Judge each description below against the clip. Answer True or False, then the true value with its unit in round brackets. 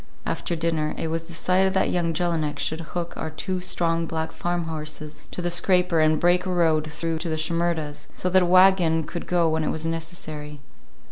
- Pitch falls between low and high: True (165 Hz)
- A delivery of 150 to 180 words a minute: False (195 wpm)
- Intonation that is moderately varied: False (1.9 semitones)